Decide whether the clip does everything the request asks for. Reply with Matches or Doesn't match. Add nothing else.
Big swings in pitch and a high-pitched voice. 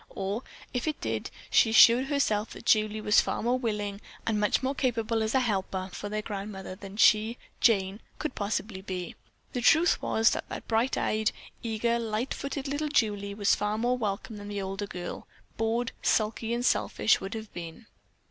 Doesn't match